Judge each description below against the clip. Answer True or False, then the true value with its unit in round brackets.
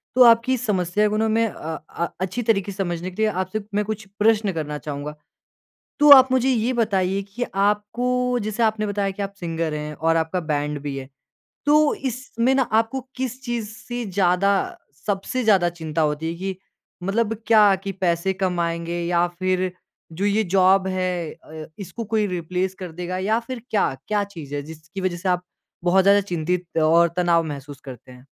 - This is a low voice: False (190 Hz)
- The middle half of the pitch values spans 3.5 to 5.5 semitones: True (4.3 semitones)